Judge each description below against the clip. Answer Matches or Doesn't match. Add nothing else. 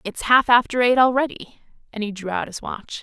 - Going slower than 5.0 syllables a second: Doesn't match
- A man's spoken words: Doesn't match